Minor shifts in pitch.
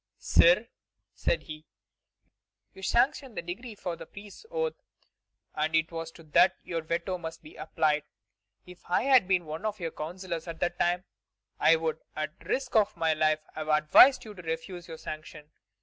No: average, 3.4 semitones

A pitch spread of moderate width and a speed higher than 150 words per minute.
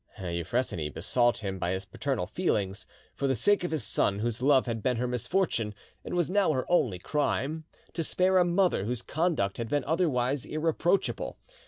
No: wide, 7.6 semitones; average, 180 wpm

